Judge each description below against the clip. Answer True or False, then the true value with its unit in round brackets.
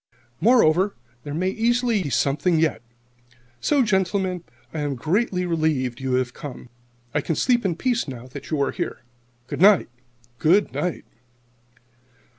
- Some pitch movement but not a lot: False (6.1 semitones)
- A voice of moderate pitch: True (175 Hz)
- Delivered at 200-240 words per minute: False (145 wpm)